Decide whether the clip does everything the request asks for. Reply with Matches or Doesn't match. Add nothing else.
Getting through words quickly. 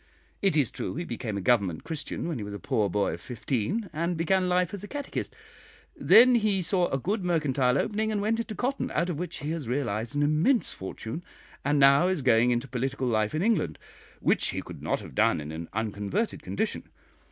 Matches